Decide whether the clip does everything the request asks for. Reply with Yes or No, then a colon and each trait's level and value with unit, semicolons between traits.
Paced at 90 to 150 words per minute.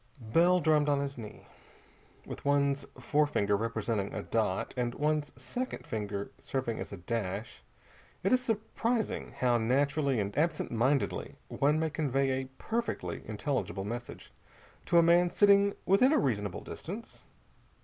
Yes: average, 140 wpm